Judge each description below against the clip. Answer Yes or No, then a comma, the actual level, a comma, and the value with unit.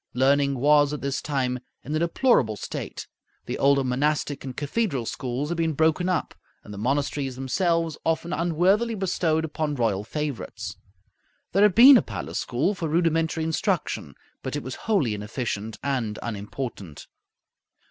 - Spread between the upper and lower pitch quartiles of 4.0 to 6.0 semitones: Yes, average, 4.7 semitones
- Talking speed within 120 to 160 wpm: Yes, average, 150 wpm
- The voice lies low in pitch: No, medium, 145 Hz